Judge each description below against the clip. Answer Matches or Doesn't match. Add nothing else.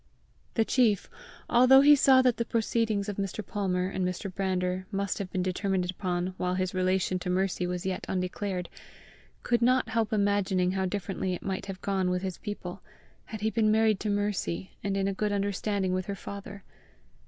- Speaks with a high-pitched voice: Matches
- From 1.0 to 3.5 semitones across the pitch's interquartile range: Matches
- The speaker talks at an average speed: Matches